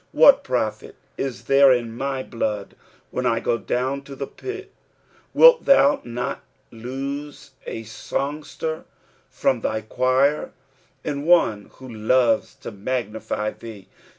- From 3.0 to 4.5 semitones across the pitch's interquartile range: Yes, average, 3.7 semitones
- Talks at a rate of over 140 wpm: No, slow, 135 wpm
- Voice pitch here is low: Yes, low, 130 Hz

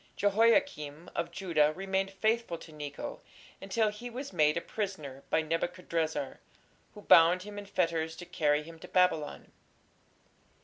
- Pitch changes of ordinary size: Yes, average, 4.5 semitones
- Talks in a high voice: No, medium, 175 Hz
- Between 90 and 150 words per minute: Yes, average, 145 wpm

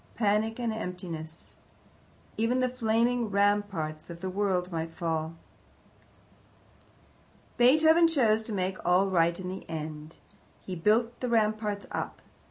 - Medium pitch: No, high, 200 Hz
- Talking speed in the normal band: No, slow, 125 wpm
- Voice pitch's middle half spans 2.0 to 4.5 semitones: No, average, 4.9 semitones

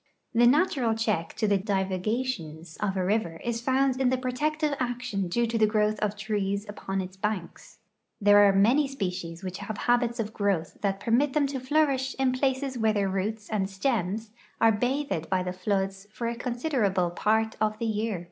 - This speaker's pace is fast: No, average, 185 wpm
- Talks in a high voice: Yes, high, 215 Hz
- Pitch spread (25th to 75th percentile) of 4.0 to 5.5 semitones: Yes, average, 4.4 semitones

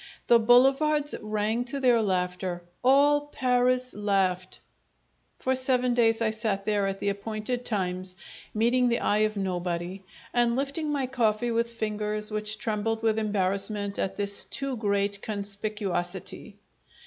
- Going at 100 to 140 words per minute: Yes, slow, 135 wpm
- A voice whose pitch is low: No, high, 215 Hz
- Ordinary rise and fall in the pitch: Yes, average, 3.6 semitones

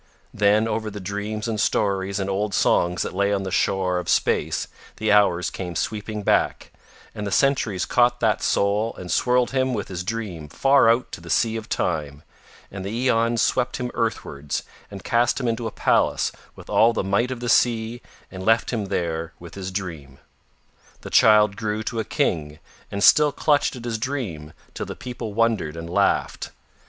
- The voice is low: Yes, low, 105 Hz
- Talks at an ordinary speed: Yes, average, 190 wpm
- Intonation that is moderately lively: Yes, average, 3.7 semitones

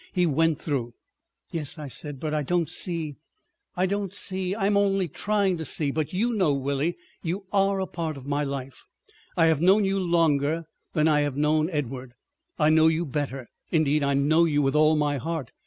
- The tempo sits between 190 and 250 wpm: Yes, average, 195 wpm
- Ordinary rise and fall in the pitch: Yes, average, 3.8 semitones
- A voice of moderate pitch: Yes, medium, 155 Hz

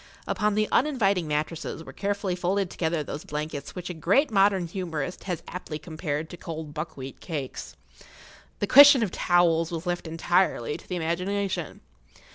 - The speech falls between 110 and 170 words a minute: Yes, average, 160 wpm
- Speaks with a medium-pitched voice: Yes, medium, 175 Hz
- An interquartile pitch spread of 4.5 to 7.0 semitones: No, average, 3.6 semitones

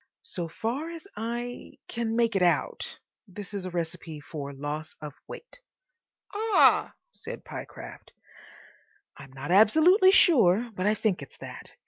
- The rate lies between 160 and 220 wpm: No, slow, 135 wpm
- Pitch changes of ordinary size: No, wide, 6.7 semitones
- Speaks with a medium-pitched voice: No, high, 205 Hz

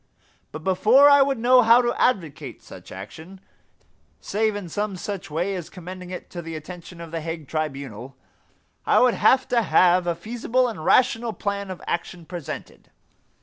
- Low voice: No, medium, 185 Hz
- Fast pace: No, average, 170 wpm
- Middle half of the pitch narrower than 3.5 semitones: No, wide, 5.6 semitones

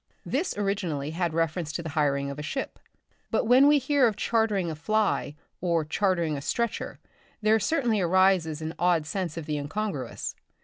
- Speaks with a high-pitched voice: No, medium, 175 Hz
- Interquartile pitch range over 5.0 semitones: Yes, wide, 5.5 semitones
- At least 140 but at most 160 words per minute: No, average, 175 wpm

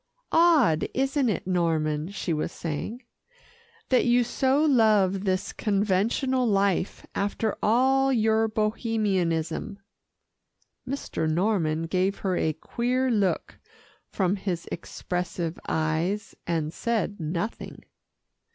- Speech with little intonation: No, wide, 5.4 semitones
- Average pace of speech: No, slow, 105 wpm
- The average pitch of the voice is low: No, high, 200 Hz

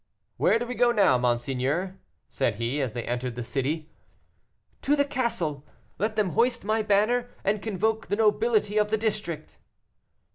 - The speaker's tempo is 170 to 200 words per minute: No, average, 160 wpm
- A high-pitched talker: Yes, high, 205 Hz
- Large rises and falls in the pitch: Yes, wide, 8.0 semitones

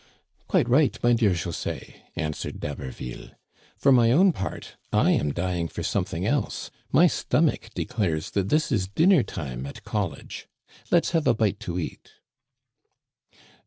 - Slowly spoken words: No, average, 150 wpm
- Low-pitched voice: Yes, low, 100 Hz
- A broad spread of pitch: Yes, wide, 7.0 semitones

